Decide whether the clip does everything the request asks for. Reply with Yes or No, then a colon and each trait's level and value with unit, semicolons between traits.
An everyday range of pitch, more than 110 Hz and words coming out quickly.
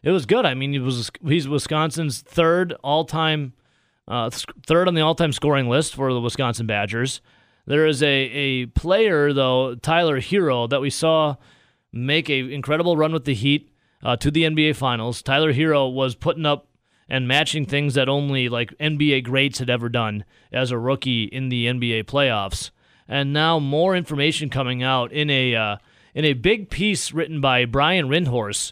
No: average, 3.4 semitones; medium, 140 Hz; average, 180 wpm